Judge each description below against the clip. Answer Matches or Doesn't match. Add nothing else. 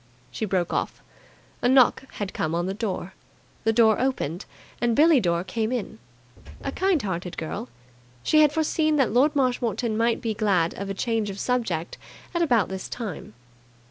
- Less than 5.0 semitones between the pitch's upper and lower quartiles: Doesn't match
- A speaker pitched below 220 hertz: Doesn't match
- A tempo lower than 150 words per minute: Doesn't match